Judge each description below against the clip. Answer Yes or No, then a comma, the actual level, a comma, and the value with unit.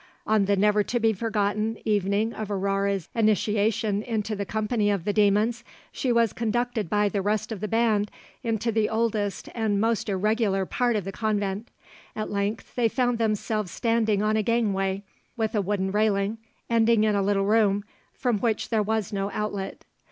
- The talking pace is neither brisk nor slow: Yes, average, 175 wpm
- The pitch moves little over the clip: Yes, narrow, 1.9 semitones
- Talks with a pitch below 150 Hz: No, high, 215 Hz